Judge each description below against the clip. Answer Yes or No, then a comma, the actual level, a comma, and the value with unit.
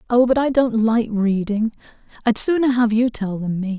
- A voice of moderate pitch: No, high, 225 Hz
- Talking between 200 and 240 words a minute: Yes, fast, 205 wpm